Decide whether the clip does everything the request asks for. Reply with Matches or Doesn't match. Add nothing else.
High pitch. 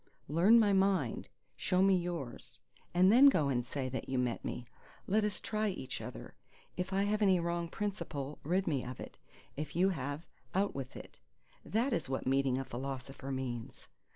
Doesn't match